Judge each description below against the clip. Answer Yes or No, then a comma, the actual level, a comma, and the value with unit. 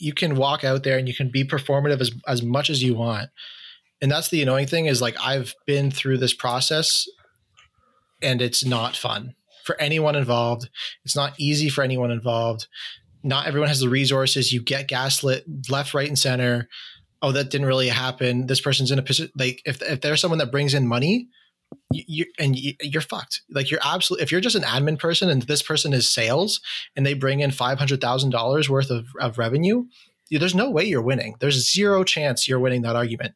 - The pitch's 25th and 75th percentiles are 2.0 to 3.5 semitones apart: Yes, average, 2.9 semitones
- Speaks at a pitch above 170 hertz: No, low, 135 Hz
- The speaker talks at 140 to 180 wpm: No, fast, 205 wpm